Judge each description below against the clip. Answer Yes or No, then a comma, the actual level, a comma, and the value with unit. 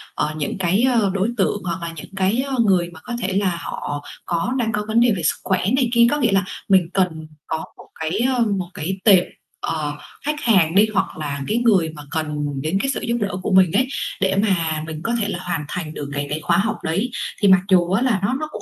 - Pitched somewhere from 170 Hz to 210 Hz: Yes, high, 190 Hz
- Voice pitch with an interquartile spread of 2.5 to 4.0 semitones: No, average, 5.1 semitones